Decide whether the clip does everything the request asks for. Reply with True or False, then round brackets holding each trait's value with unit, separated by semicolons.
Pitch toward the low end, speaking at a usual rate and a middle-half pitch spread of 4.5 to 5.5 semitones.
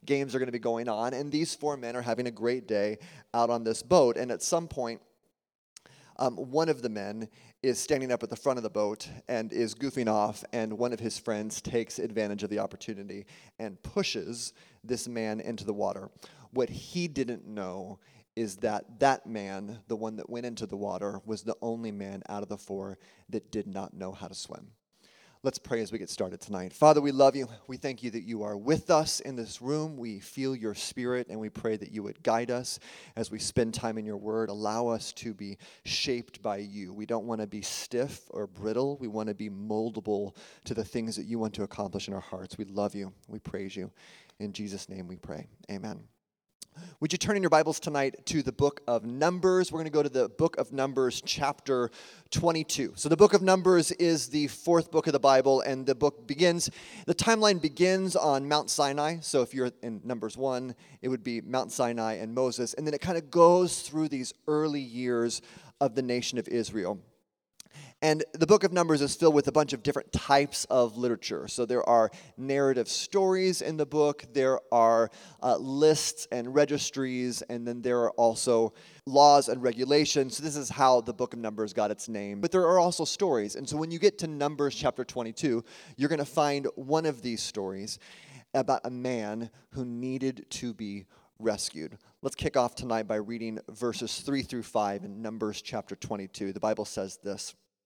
False (120 Hz; 210 wpm; 4.9 semitones)